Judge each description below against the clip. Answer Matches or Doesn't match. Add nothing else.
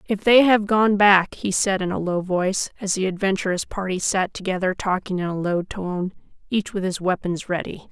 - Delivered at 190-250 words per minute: Matches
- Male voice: Doesn't match